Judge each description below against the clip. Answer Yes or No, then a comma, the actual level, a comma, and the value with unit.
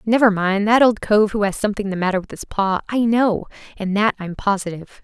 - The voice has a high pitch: Yes, high, 205 Hz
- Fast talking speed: Yes, fast, 225 wpm